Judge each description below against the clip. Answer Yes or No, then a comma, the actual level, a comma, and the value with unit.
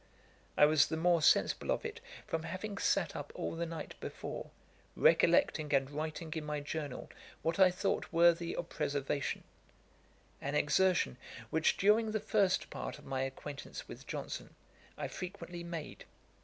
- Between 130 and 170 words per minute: Yes, average, 155 wpm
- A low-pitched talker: No, medium, 165 Hz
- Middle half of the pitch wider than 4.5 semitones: No, average, 3.4 semitones